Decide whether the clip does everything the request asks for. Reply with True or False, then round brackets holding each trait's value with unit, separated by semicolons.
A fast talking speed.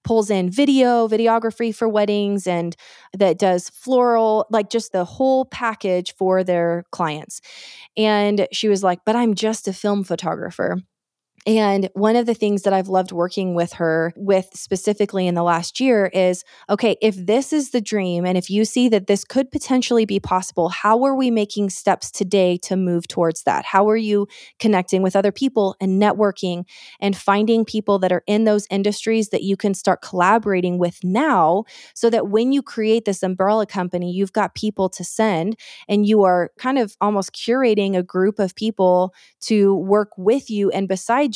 False (185 wpm)